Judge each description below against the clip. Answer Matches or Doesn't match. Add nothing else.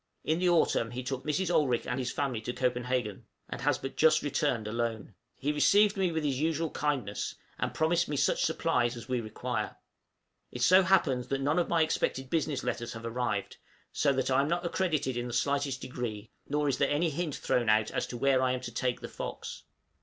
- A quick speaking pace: Matches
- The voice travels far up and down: Doesn't match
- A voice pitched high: Doesn't match